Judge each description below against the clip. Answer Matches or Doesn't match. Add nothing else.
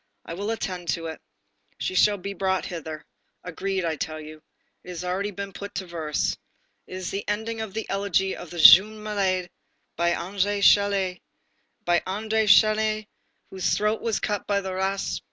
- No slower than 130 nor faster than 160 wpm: Doesn't match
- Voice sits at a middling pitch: Doesn't match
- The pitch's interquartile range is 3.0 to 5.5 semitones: Doesn't match